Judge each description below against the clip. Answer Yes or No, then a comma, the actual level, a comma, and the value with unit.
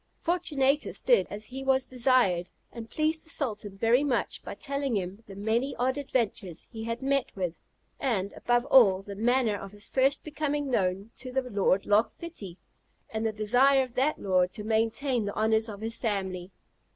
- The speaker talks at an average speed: Yes, average, 180 wpm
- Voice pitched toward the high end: Yes, high, 230 Hz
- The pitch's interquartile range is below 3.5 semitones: No, average, 4.7 semitones